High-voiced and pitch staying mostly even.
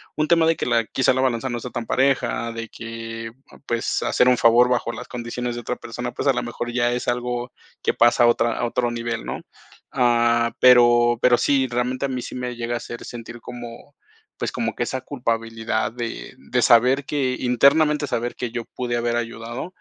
No: low, 120 Hz; narrow, 1.3 semitones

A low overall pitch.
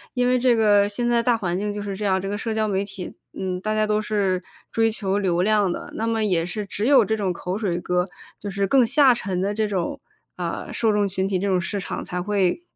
No: high, 205 Hz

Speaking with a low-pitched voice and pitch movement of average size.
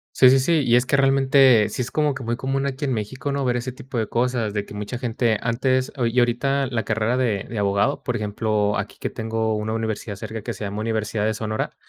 Yes: low, 115 Hz; average, 3.2 semitones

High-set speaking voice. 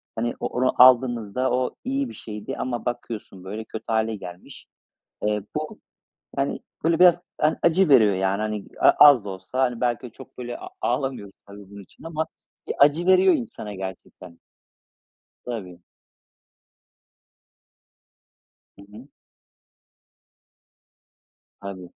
No: low, 120 Hz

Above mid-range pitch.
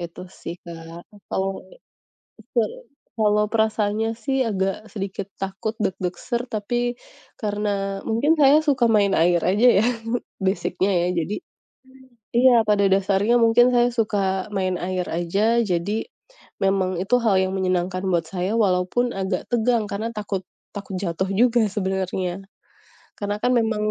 Yes: high, 200 Hz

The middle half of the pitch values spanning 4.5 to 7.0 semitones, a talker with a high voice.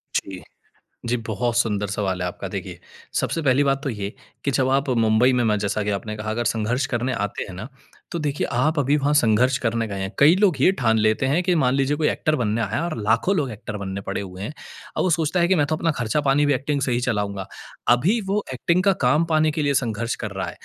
No: wide, 5.5 semitones; low, 125 Hz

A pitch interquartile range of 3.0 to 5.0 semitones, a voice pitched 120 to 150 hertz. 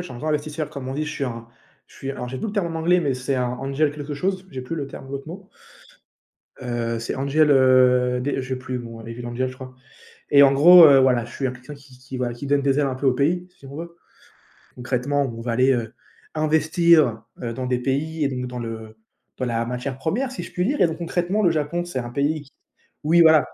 Yes: average, 3.7 semitones; low, 135 Hz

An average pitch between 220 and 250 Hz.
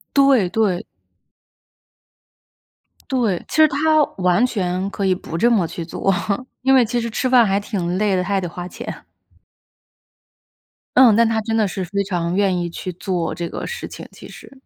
No: high, 200 Hz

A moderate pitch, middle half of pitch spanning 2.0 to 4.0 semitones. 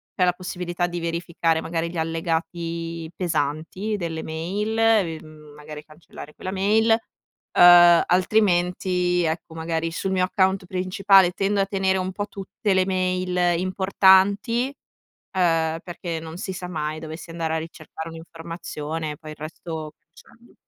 Yes: medium, 175 Hz; narrow, 2.6 semitones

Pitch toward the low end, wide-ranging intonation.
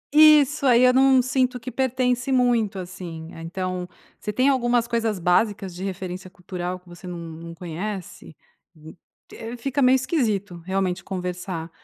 No: high, 195 Hz; wide, 5.9 semitones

